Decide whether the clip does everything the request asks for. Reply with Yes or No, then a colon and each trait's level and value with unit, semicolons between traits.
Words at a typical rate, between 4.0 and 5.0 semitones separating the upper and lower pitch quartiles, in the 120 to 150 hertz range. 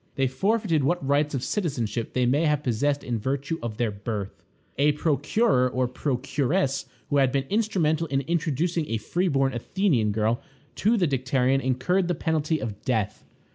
Yes: average, 170 wpm; average, 4.6 semitones; medium, 140 Hz